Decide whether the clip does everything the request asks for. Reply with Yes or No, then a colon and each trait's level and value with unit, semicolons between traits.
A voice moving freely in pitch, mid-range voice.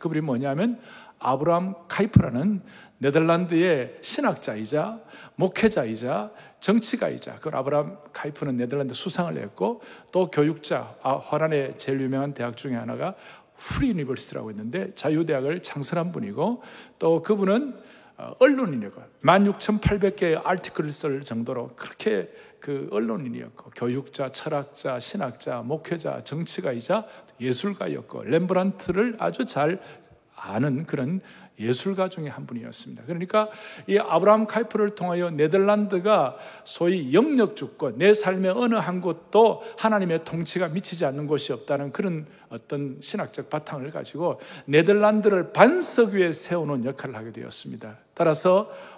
Yes: wide, 6.4 semitones; medium, 175 Hz